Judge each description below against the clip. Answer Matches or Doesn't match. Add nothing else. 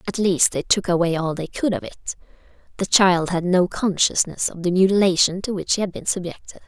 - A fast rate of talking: Matches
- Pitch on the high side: Doesn't match